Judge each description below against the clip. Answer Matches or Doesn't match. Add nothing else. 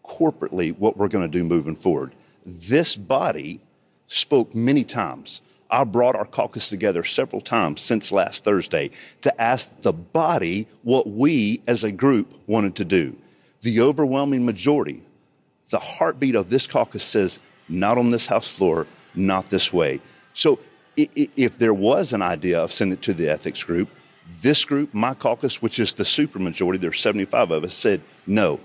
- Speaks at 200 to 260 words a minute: Doesn't match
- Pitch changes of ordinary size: Doesn't match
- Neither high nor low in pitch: Doesn't match